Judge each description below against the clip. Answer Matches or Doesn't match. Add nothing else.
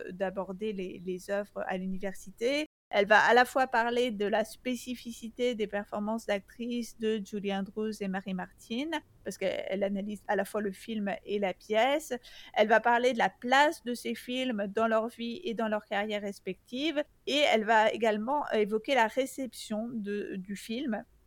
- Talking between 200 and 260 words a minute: Doesn't match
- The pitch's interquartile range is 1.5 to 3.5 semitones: Matches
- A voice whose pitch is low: Doesn't match